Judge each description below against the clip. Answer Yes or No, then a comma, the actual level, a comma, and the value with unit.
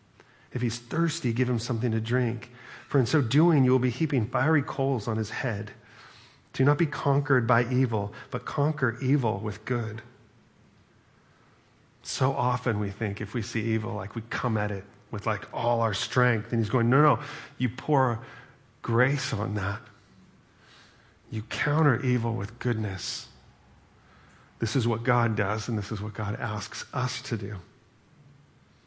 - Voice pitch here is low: Yes, low, 120 Hz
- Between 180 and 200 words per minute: No, average, 165 wpm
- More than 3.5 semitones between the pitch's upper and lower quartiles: No, average, 3.0 semitones